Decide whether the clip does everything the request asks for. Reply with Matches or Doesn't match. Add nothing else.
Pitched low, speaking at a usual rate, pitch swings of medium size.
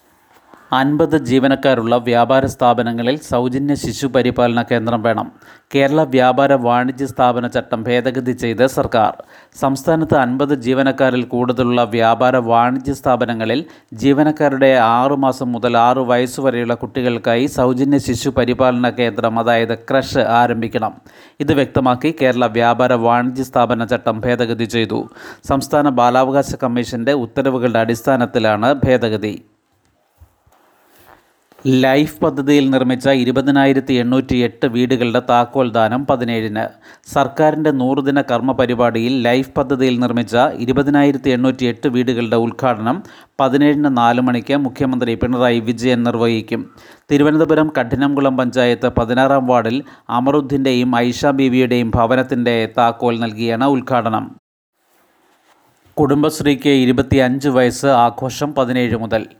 Doesn't match